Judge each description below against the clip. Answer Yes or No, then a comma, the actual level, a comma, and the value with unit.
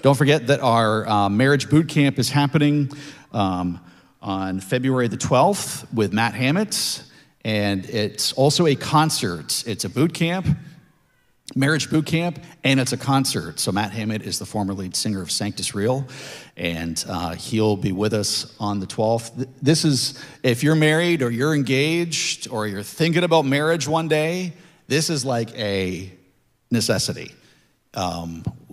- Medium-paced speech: Yes, average, 155 wpm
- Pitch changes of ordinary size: No, wide, 6.6 semitones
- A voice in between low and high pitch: No, low, 130 Hz